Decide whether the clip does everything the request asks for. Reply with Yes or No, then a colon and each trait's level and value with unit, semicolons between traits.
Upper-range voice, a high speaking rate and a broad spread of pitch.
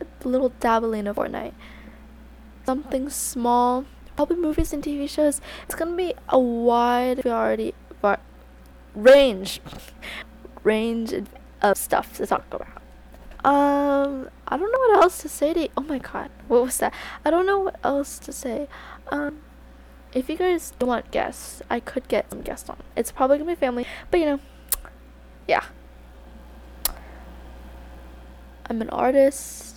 No: very high, 255 Hz; average, 150 wpm; wide, 6.1 semitones